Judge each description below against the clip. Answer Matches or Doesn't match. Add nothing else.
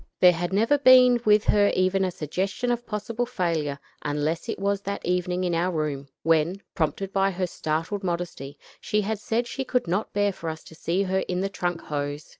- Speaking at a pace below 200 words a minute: Doesn't match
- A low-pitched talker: Doesn't match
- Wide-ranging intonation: Doesn't match